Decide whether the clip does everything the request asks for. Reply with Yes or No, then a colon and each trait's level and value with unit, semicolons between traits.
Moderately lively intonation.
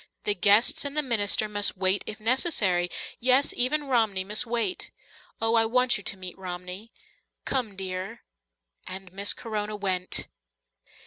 Yes: average, 4.0 semitones